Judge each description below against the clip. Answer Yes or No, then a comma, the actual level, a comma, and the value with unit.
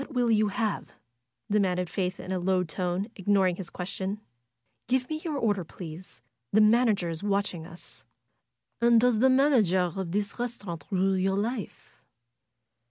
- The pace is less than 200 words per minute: Yes, average, 155 wpm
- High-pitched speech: Yes, high, 200 Hz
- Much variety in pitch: No, average, 4.0 semitones